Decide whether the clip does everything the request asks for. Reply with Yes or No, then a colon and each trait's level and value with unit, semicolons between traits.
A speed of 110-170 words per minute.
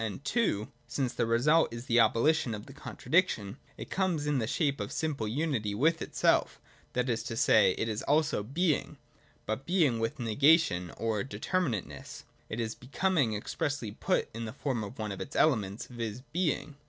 No: average, 180 wpm